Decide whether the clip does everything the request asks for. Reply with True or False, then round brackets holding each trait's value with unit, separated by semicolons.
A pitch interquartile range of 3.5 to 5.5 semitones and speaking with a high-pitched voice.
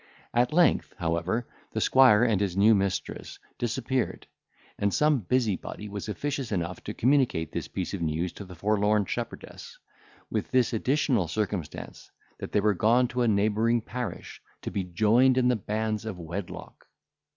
False (4.1 semitones; 110 Hz)